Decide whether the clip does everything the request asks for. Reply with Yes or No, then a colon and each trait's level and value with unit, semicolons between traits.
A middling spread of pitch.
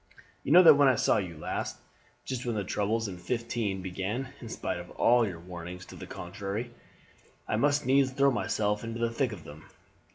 Yes: average, 5.0 semitones